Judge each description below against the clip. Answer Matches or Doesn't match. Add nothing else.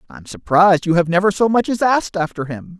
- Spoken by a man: Matches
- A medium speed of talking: Doesn't match